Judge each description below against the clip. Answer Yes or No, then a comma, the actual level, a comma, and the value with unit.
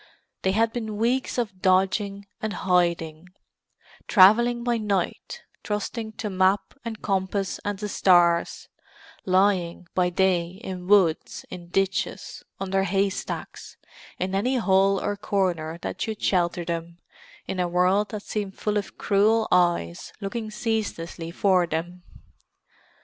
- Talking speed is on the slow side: Yes, slow, 130 wpm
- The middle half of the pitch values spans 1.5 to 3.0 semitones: Yes, average, 2.7 semitones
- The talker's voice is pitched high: Yes, high, 195 Hz